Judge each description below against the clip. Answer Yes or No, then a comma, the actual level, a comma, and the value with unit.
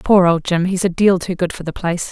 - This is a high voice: No, medium, 180 Hz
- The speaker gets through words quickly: Yes, fast, 315 wpm